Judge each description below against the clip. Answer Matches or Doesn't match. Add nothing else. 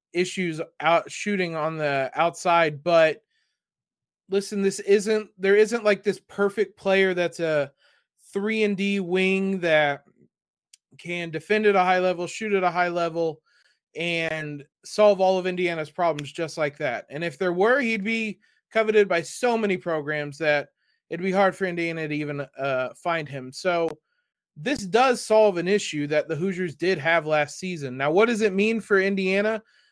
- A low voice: Doesn't match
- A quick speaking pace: Doesn't match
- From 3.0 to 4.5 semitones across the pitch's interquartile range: Matches